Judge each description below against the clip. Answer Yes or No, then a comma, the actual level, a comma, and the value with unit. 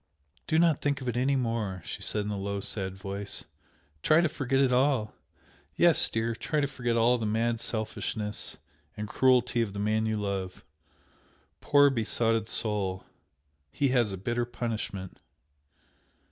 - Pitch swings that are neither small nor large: Yes, average, 3.5 semitones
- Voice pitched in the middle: No, low, 115 Hz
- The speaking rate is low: No, average, 160 wpm